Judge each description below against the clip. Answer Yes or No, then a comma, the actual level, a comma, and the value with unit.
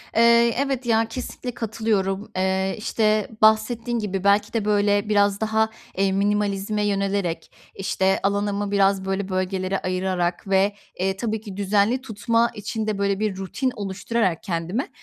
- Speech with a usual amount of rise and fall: No, narrow, 2.3 semitones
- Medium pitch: No, high, 205 Hz